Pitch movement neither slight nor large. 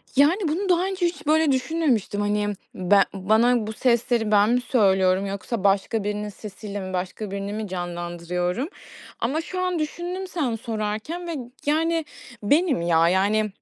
No: wide, 7.6 semitones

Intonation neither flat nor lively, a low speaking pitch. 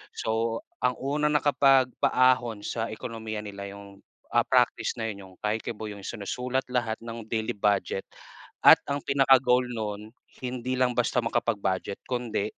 Yes: average, 3.2 semitones; low, 115 Hz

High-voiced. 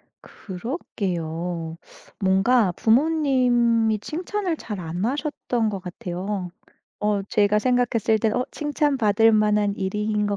Yes: high, 215 Hz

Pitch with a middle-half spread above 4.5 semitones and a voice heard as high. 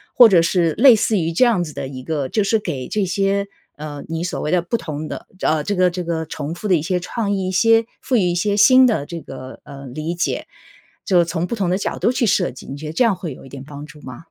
No: average, 4.9 semitones; medium, 175 Hz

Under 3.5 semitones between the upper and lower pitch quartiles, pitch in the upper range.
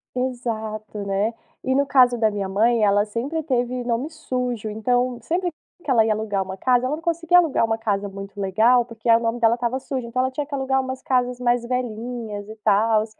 Yes: average, 3.0 semitones; high, 240 Hz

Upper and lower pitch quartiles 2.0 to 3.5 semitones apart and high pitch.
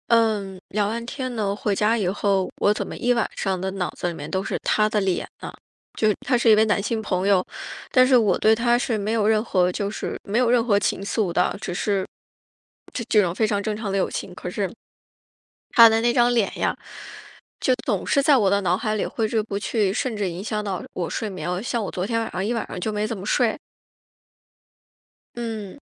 Yes: average, 2.9 semitones; high, 210 Hz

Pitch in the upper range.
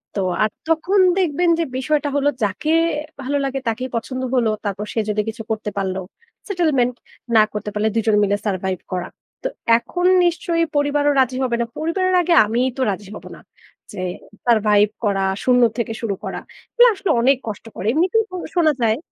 Yes: very high, 250 Hz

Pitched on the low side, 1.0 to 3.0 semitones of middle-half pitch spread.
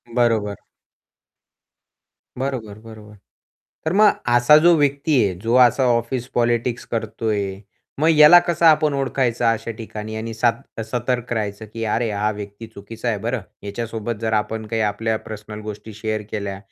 Yes: low, 115 Hz; narrow, 2.4 semitones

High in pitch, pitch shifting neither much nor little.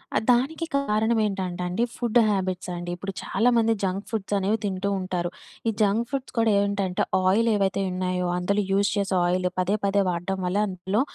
Yes: high, 195 Hz; average, 3.0 semitones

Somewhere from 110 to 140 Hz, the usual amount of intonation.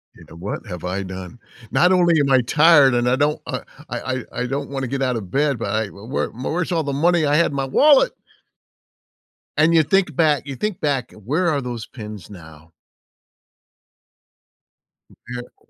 No: low, 135 Hz; wide, 6.0 semitones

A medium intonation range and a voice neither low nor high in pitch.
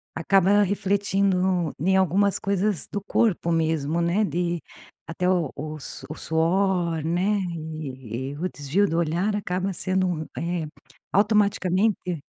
Yes: average, 3.4 semitones; medium, 180 Hz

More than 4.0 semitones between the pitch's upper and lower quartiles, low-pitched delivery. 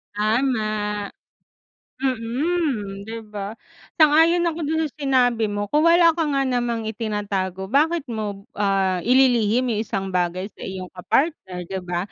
No: wide, 5.5 semitones; high, 225 Hz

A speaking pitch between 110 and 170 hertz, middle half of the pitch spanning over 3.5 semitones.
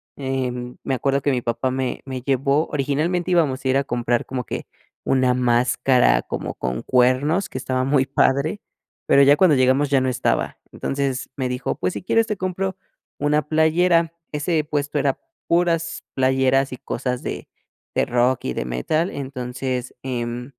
No: low, 135 Hz; average, 2.9 semitones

